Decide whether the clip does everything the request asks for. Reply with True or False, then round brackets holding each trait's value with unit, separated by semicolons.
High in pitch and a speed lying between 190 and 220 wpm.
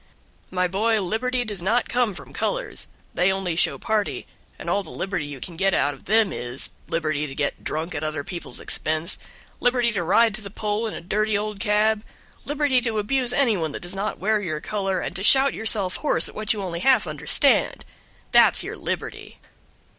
True (200 Hz; 200 wpm)